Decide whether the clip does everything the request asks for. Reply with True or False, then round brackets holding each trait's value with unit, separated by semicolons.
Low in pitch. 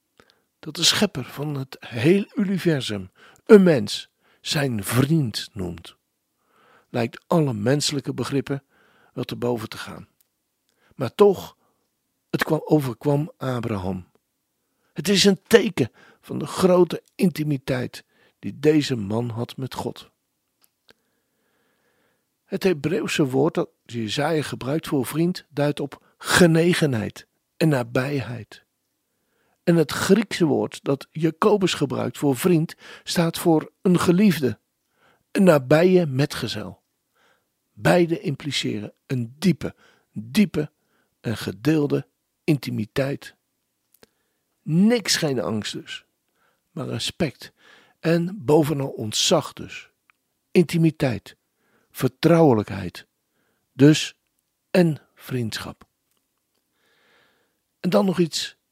False (150 Hz)